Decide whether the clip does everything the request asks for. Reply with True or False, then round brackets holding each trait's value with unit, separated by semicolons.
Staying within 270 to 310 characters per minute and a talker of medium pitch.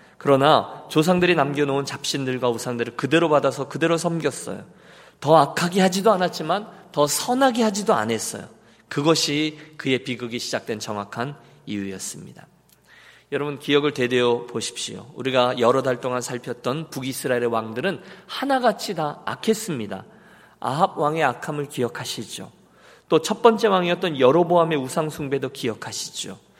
False (345 characters per minute; 145 Hz)